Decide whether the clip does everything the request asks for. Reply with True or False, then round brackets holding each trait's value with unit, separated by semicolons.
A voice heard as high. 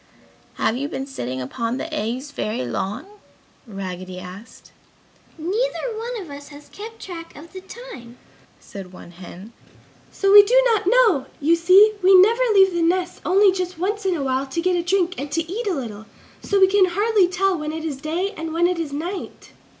True (335 Hz)